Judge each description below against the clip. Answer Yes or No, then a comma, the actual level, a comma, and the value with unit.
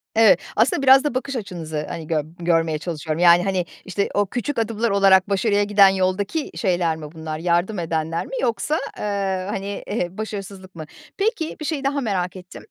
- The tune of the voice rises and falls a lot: No, average, 4.6 semitones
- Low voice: No, high, 195 Hz